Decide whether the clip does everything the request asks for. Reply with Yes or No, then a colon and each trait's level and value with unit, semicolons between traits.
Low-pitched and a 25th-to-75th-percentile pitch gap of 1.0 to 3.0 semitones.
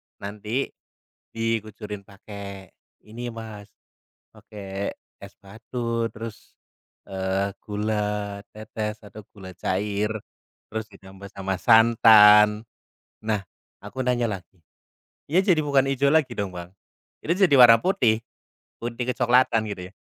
Yes: low, 105 Hz; narrow, 2.6 semitones